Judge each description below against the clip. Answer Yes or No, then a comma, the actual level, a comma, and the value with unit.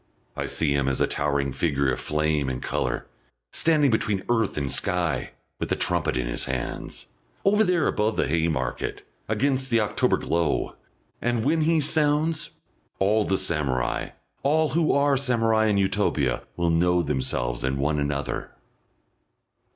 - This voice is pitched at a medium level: No, very low, 95 Hz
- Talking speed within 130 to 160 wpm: Yes, average, 150 wpm